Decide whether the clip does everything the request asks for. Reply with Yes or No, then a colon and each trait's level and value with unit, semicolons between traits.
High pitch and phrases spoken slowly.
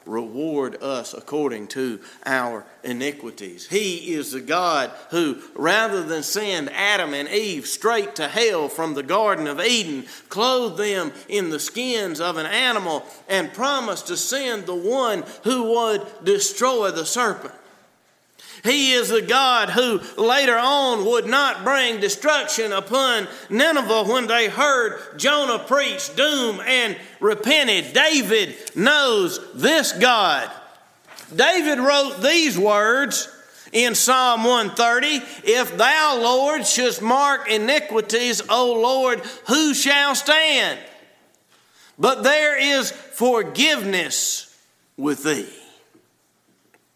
Yes: high, 245 Hz; slow, 120 wpm